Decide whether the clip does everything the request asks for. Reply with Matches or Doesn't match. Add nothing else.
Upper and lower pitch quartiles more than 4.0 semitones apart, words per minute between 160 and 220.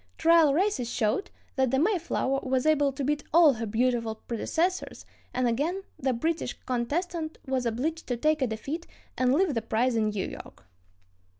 Matches